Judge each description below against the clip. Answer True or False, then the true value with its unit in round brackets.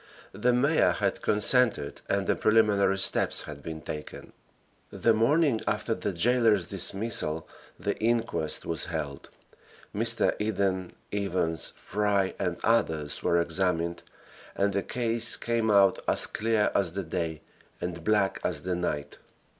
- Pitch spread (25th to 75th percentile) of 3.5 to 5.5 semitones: True (4.8 semitones)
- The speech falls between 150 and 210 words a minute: False (135 wpm)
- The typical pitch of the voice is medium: False (100 Hz)